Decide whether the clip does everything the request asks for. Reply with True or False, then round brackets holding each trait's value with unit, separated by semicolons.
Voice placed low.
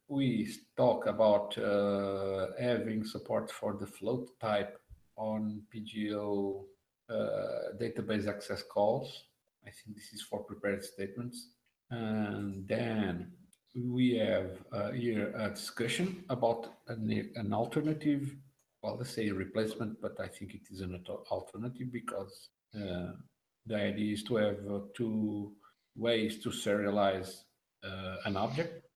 True (110 Hz)